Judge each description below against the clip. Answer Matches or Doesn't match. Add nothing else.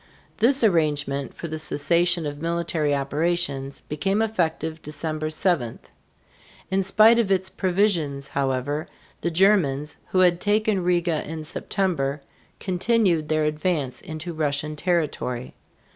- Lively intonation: Doesn't match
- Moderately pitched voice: Matches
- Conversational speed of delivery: Doesn't match